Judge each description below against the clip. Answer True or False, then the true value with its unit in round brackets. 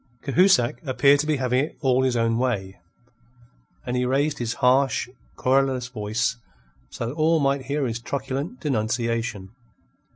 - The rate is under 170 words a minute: True (150 wpm)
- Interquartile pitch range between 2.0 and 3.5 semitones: True (2.9 semitones)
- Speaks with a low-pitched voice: True (130 Hz)